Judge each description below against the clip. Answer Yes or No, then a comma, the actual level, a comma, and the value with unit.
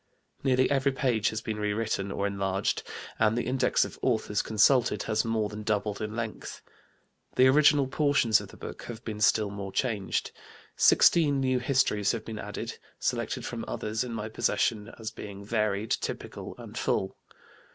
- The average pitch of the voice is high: No, low, 110 Hz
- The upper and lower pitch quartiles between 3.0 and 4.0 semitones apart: Yes, average, 3.4 semitones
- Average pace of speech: Yes, average, 165 wpm